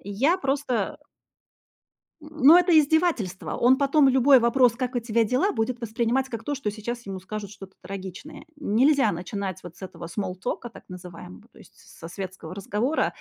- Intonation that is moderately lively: No, wide, 5.7 semitones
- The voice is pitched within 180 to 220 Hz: No, high, 235 Hz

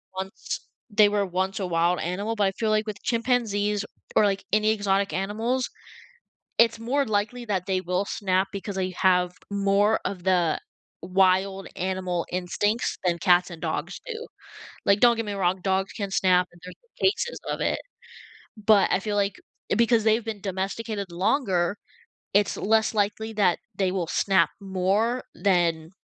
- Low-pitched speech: No, high, 195 Hz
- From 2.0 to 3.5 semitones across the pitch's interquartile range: Yes, narrow, 2.6 semitones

